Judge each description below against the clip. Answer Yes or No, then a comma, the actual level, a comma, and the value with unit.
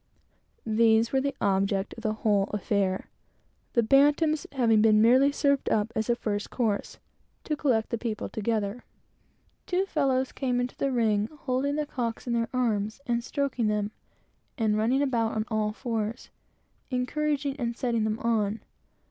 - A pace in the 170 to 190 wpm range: No, average, 160 wpm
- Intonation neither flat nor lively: Yes, average, 3.5 semitones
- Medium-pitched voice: No, high, 230 Hz